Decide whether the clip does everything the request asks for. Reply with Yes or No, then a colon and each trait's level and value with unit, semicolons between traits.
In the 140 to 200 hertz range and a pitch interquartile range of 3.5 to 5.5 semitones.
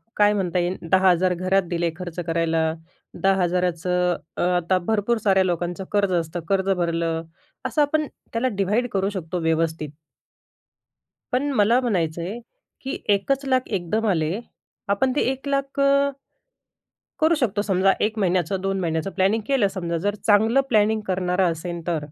Yes: high, 190 Hz; average, 4.0 semitones